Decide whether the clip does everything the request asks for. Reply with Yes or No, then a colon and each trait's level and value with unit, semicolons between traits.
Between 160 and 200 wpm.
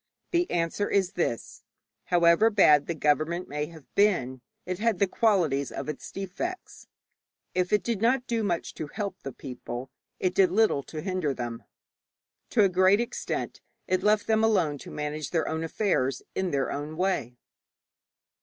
Yes: average, 165 wpm